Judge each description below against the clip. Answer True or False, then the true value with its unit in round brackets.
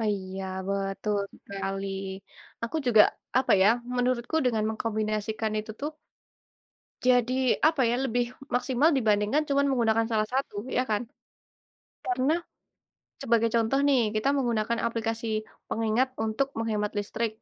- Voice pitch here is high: True (225 Hz)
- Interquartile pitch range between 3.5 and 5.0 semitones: False (2.8 semitones)